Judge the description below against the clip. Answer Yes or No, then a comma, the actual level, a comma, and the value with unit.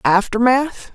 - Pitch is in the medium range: No, high, 235 Hz